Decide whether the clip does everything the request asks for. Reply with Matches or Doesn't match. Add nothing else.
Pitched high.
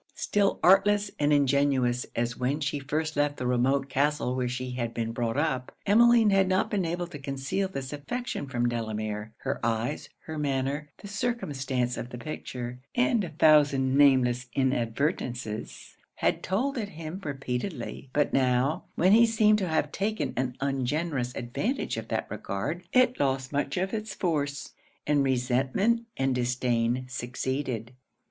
Doesn't match